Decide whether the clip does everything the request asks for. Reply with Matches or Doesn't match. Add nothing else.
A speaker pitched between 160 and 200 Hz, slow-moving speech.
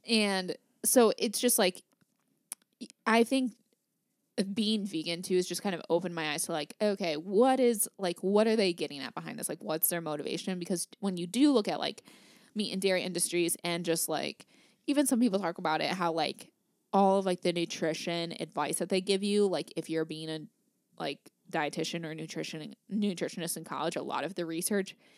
Doesn't match